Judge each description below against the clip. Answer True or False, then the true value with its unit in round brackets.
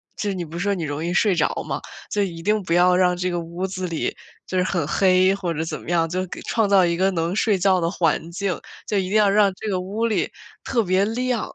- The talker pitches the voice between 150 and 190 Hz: True (185 Hz)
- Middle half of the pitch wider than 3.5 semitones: False (2.7 semitones)